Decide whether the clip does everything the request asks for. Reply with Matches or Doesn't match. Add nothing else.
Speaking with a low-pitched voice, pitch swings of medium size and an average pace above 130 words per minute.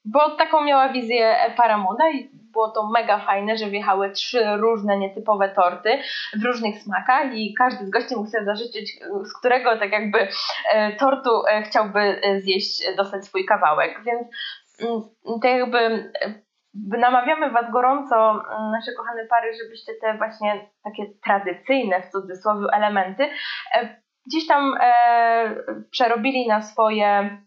Doesn't match